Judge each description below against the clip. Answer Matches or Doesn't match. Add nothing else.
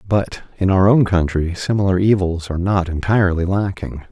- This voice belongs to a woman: Doesn't match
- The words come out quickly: Doesn't match